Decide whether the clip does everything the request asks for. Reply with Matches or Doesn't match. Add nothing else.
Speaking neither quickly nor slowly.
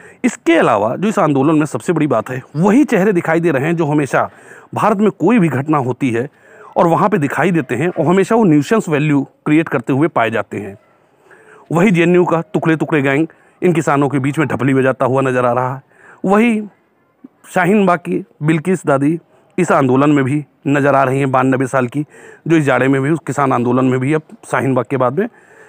Doesn't match